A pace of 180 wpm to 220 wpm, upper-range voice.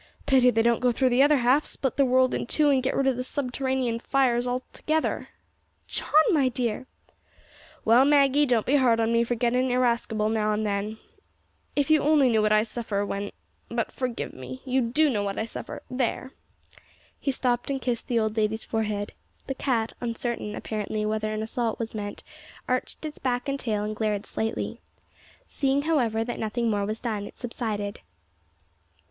Yes: average, 185 wpm; high, 240 Hz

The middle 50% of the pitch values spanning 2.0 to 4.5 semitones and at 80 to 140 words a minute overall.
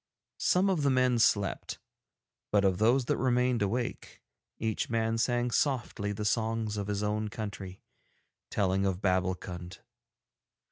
Yes: average, 3.6 semitones; slow, 135 wpm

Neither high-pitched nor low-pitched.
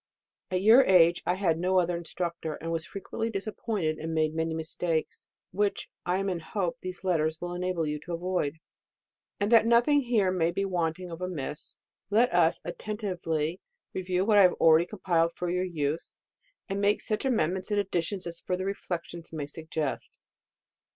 Yes: medium, 180 Hz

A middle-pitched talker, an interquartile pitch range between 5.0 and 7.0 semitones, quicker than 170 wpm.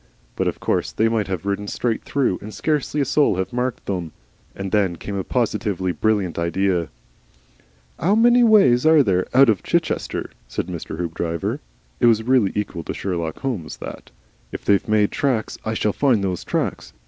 No: low, 105 Hz; average, 5.3 semitones; average, 180 wpm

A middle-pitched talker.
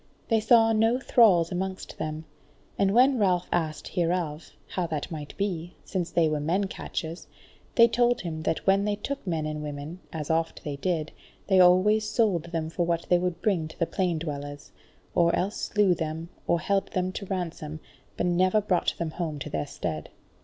Yes: medium, 175 Hz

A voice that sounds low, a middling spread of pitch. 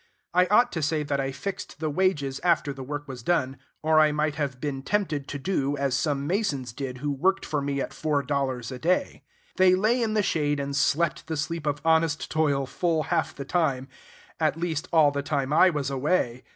No: medium, 150 Hz; average, 3.1 semitones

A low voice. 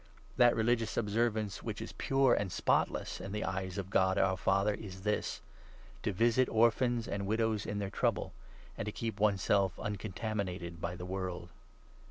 Yes: low, 100 Hz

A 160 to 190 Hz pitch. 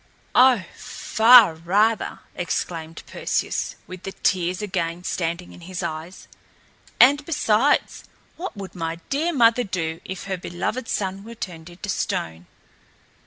Yes: medium, 185 Hz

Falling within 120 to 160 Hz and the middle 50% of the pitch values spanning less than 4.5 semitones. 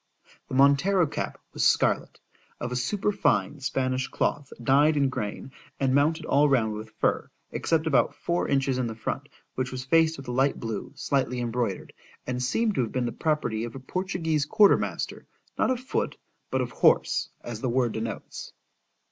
Yes: low, 135 Hz; average, 4.1 semitones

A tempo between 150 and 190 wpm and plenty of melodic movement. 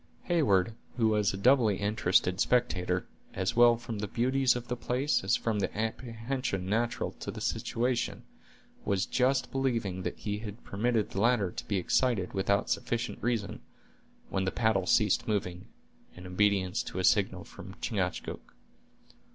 No: average, 155 wpm; average, 3.9 semitones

